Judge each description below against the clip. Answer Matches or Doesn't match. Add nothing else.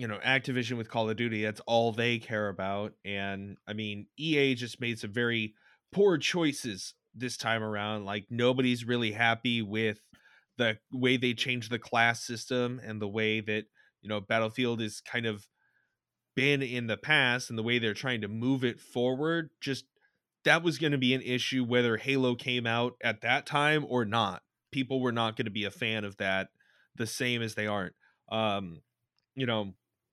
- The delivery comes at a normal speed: Matches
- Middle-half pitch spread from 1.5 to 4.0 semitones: Matches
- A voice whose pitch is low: Matches